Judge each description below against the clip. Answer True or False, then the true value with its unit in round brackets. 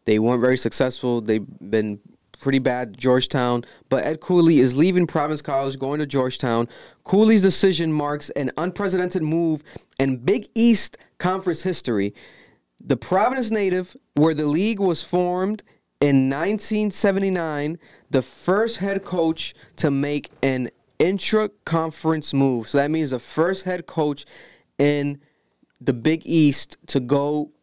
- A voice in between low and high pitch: True (155 Hz)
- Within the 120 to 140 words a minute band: True (135 wpm)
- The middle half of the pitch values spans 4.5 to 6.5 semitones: True (5.2 semitones)